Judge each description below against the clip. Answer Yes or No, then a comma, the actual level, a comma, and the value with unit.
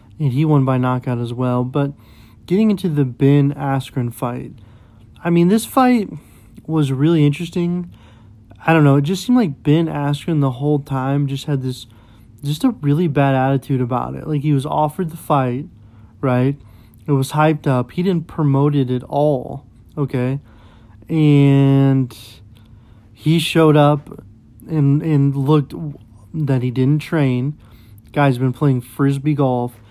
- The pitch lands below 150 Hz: Yes, medium, 140 Hz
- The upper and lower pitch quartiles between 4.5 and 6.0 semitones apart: No, average, 3.7 semitones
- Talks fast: No, average, 155 wpm